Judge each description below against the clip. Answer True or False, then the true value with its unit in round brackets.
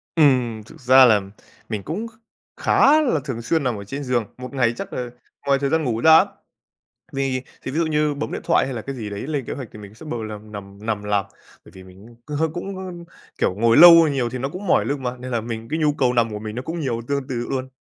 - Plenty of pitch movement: False (4.7 semitones)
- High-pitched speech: False (130 Hz)